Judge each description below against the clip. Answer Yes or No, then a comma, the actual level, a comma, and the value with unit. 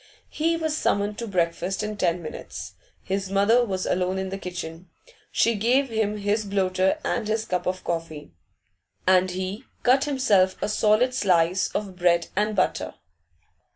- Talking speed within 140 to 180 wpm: Yes, average, 155 wpm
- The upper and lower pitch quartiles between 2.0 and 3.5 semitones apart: Yes, average, 3.0 semitones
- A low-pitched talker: No, high, 195 Hz